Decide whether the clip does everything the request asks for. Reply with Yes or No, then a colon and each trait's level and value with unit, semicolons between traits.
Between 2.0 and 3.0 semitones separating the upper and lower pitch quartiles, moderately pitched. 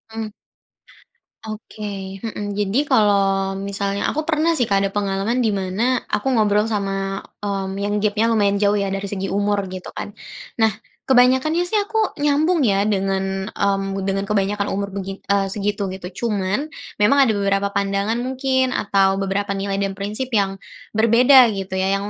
No: narrow, 2.4 semitones; high, 200 Hz